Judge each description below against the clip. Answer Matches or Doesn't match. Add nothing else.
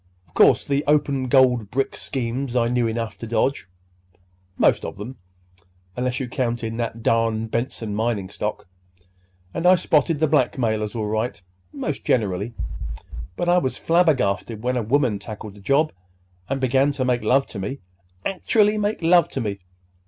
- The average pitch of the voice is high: Doesn't match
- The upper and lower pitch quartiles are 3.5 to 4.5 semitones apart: Matches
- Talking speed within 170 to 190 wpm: Doesn't match